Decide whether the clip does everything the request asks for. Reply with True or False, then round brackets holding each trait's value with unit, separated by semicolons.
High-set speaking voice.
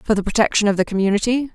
True (215 Hz)